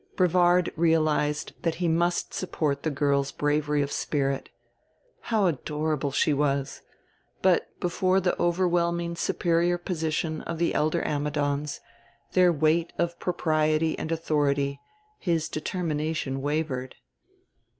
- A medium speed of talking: No, slow, 115 wpm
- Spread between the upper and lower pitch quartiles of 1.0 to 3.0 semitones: Yes, average, 2.7 semitones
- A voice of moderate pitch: Yes, medium, 155 Hz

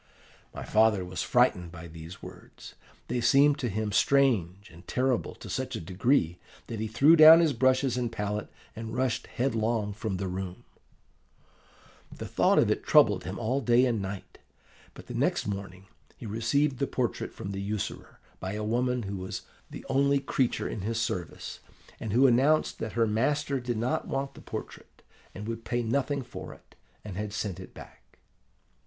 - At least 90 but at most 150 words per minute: No, average, 180 wpm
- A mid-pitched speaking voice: No, low, 115 Hz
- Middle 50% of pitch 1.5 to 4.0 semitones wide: No, average, 4.6 semitones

